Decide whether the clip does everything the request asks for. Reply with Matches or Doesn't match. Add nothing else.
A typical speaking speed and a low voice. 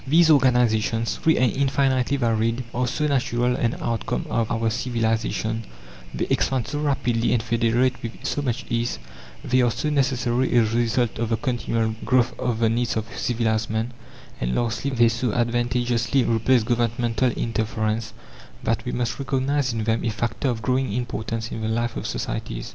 Matches